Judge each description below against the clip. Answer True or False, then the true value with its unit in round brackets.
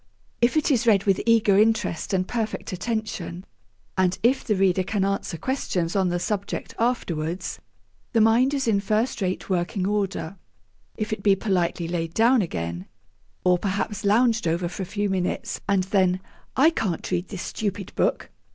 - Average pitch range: True (3.5 semitones)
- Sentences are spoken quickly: False (170 wpm)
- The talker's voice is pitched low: False (195 Hz)